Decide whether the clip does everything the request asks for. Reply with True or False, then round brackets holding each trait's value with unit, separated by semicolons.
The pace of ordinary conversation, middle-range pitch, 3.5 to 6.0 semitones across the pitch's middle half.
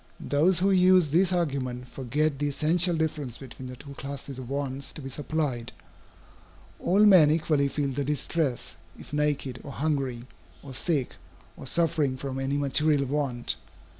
False (155 wpm; 145 Hz; 2.9 semitones)